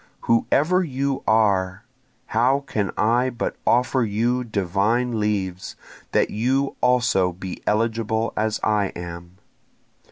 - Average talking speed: No, slow, 115 wpm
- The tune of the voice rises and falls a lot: No, average, 3.9 semitones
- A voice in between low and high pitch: No, low, 110 Hz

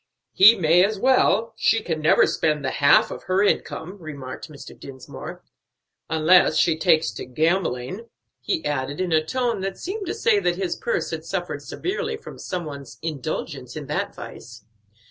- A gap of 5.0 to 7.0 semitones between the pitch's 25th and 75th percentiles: Yes, wide, 5.5 semitones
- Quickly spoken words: No, average, 170 wpm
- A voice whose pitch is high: No, medium, 175 Hz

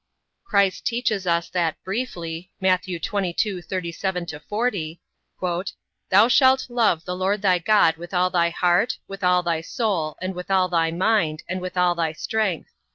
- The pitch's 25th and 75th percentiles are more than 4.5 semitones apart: No, average, 2.9 semitones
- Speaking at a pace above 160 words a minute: No, average, 155 wpm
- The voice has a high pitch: No, medium, 180 Hz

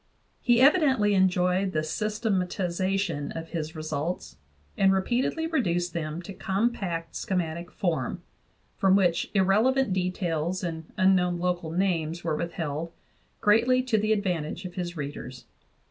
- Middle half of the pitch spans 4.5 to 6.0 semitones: No, average, 3.3 semitones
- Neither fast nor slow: No, slow, 130 wpm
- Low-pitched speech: No, medium, 180 Hz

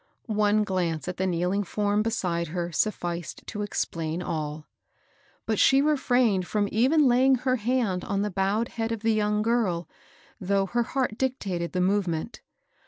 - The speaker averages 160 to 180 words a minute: Yes, average, 165 wpm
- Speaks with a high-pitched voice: Yes, high, 205 Hz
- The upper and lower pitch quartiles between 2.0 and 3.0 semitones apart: No, average, 4.3 semitones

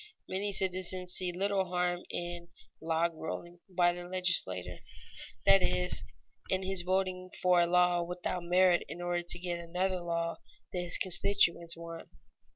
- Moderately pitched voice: Yes, medium, 180 Hz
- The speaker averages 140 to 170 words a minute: Yes, average, 150 wpm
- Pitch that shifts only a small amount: Yes, narrow, 1.2 semitones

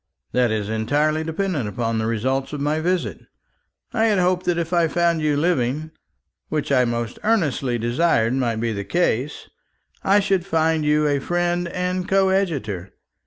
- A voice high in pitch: No, medium, 150 Hz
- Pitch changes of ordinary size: No, wide, 6.6 semitones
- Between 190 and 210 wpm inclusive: No, average, 165 wpm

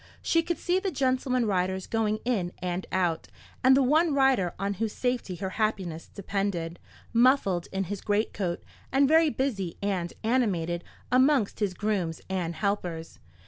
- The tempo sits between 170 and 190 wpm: No, average, 150 wpm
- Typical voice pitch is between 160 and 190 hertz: No, high, 205 Hz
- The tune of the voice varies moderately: No, wide, 5.9 semitones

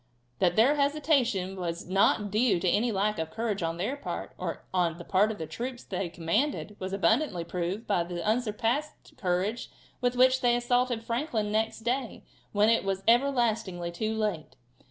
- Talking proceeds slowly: No, average, 175 wpm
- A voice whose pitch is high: Yes, high, 215 Hz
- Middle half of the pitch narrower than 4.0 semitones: No, average, 4.8 semitones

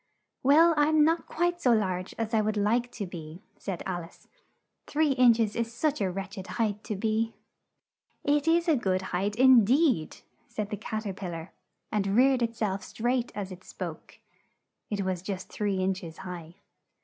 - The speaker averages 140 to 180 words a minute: No, average, 195 wpm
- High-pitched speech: Yes, high, 215 Hz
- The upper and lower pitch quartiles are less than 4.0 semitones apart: No, average, 4.8 semitones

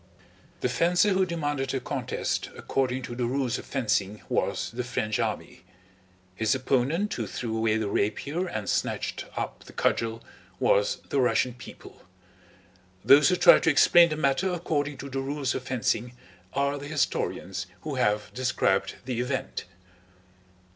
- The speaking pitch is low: Yes, low, 130 Hz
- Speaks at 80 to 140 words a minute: No, average, 155 wpm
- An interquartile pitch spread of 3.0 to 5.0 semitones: Yes, average, 3.8 semitones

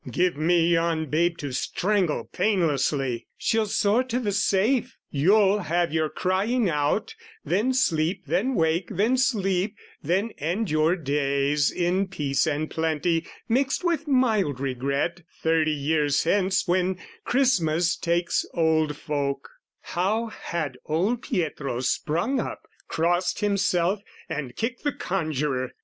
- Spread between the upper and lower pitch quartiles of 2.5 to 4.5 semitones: No, average, 5.1 semitones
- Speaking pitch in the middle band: Yes, medium, 175 Hz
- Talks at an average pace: No, slow, 130 wpm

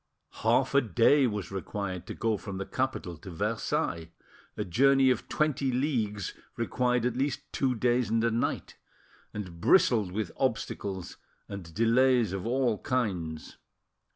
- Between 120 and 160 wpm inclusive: Yes, average, 145 wpm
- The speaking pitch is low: Yes, low, 115 Hz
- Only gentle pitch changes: No, average, 4.6 semitones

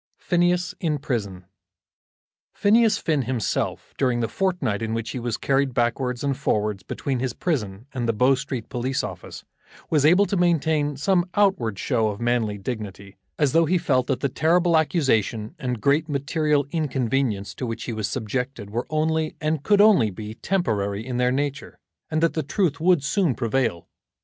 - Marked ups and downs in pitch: Yes, wide, 5.7 semitones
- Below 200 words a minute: Yes, average, 175 wpm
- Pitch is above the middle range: No, low, 135 Hz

